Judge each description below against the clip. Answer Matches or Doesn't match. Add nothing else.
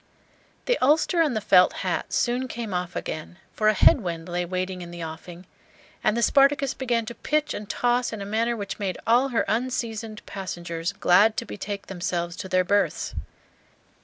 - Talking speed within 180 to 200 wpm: Matches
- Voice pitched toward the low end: Doesn't match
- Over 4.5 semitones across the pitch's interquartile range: Matches